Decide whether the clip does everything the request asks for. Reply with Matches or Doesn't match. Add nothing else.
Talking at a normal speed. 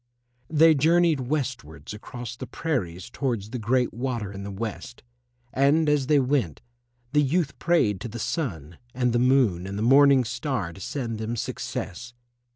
Matches